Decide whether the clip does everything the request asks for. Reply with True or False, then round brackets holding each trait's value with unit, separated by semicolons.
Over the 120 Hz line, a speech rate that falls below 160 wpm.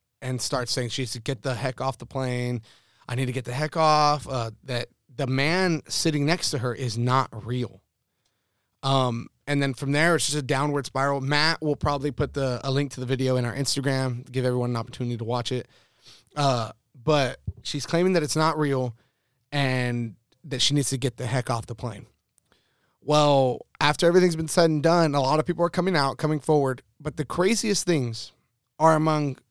False (135 Hz; 205 wpm)